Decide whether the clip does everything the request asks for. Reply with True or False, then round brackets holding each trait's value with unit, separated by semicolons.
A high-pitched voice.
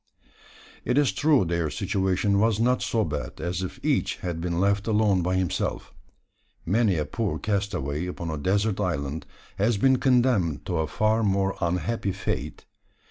False (95 Hz)